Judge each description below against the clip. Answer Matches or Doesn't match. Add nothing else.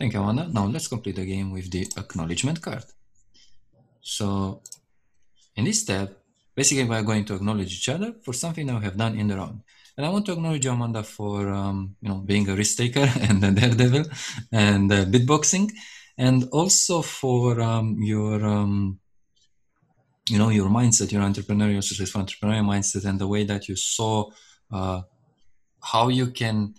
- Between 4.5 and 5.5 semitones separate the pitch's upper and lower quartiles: Doesn't match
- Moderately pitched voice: Doesn't match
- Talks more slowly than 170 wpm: Doesn't match